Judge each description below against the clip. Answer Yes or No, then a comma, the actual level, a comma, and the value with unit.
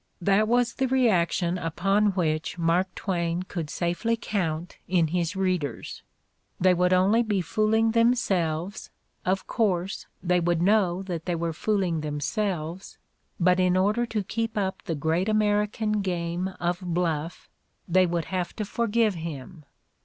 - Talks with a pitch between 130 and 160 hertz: No, medium, 185 Hz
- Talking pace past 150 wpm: No, average, 145 wpm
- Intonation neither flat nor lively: Yes, average, 3.6 semitones